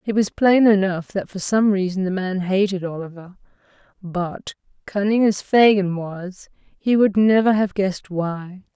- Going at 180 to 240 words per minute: No, average, 160 wpm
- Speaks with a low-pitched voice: No, high, 195 Hz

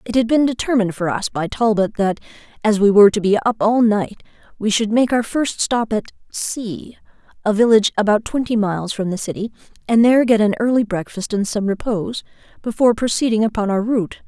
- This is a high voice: Yes, high, 215 Hz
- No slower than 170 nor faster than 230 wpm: Yes, average, 200 wpm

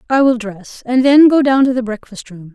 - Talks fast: Yes, fast, 260 wpm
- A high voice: Yes, high, 245 Hz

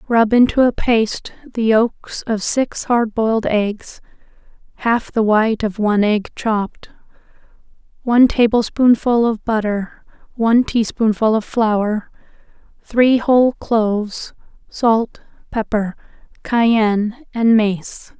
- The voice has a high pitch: Yes, high, 225 Hz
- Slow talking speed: Yes, slow, 110 wpm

